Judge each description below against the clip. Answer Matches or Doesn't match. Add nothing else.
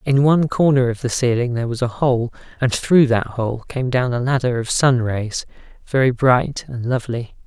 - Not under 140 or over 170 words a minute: Doesn't match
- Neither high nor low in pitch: Doesn't match